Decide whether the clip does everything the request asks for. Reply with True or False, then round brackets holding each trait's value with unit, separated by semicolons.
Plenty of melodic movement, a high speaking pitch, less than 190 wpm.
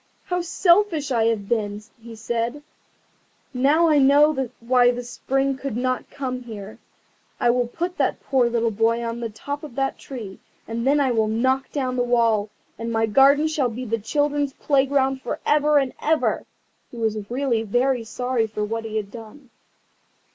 False (3.5 semitones; 245 Hz; 175 wpm)